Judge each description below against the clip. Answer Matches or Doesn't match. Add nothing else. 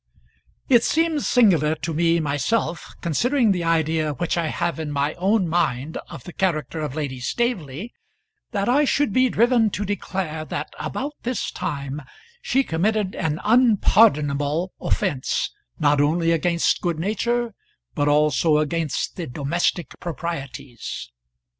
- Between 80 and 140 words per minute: Matches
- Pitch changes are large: Matches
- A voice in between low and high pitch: Matches